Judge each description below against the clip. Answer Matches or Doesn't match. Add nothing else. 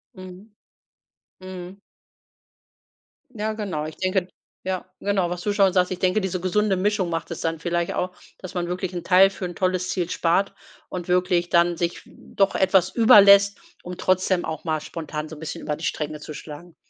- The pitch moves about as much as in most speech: Doesn't match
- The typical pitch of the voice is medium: Matches